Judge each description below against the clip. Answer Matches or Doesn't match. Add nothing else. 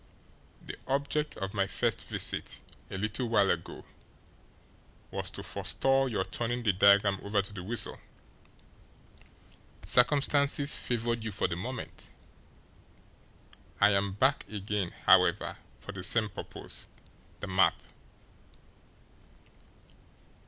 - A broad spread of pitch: Doesn't match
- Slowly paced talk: Matches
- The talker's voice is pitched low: Matches